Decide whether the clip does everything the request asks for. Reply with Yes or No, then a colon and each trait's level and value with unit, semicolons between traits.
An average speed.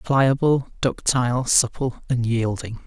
No: slow, 105 wpm